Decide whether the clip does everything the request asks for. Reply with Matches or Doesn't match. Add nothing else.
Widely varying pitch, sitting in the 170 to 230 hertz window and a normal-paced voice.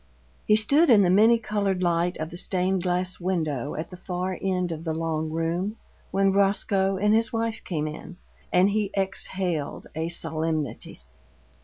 Doesn't match